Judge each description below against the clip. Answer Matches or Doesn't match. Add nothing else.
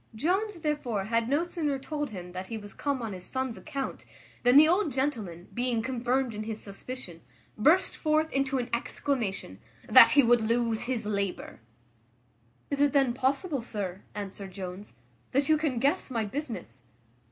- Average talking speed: Matches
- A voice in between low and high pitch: Doesn't match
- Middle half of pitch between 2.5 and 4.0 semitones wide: Doesn't match